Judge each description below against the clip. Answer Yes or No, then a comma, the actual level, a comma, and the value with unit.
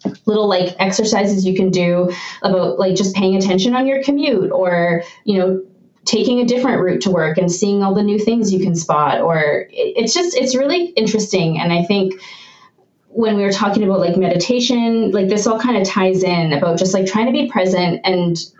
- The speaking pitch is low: No, high, 195 Hz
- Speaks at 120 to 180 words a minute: No, fast, 205 wpm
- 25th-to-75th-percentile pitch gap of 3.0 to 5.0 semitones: Yes, average, 3.3 semitones